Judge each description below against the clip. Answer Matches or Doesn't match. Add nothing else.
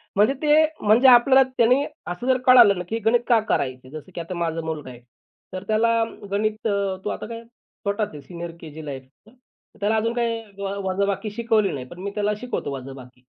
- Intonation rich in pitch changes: Matches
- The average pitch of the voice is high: Matches